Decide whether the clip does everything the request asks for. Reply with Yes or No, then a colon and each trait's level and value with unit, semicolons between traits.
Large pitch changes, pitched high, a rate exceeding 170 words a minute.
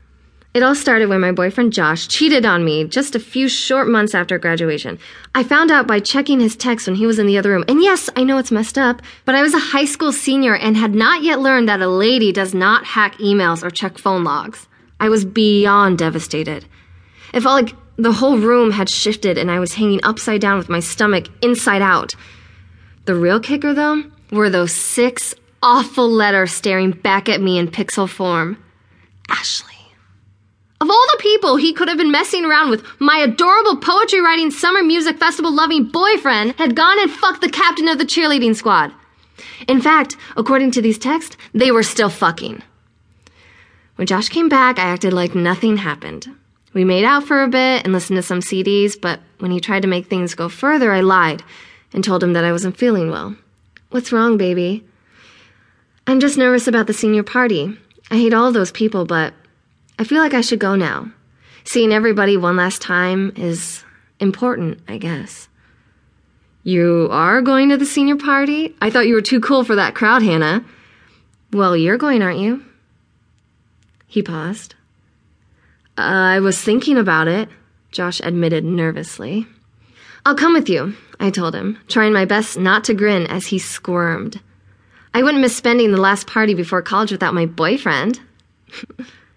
Yes: wide, 6.4 semitones; high, 210 Hz; average, 185 wpm